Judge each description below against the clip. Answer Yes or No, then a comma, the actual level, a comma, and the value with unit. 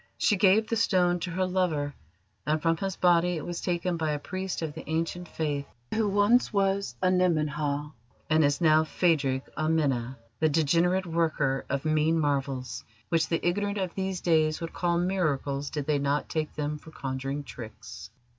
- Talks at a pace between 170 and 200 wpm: Yes, average, 175 wpm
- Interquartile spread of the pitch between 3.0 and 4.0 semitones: Yes, average, 3.7 semitones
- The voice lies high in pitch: No, medium, 160 Hz